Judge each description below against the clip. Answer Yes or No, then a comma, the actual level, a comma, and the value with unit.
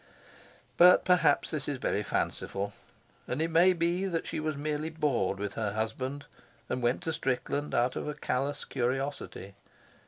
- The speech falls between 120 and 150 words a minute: No, average, 160 wpm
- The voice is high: No, medium, 145 Hz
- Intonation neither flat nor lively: Yes, average, 4.6 semitones